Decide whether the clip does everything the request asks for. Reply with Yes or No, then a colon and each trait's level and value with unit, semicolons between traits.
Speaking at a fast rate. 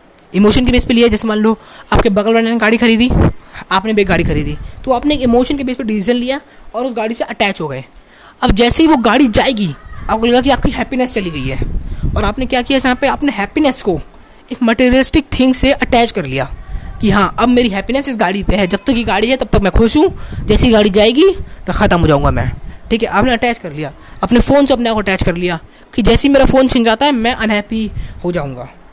Yes: fast, 245 wpm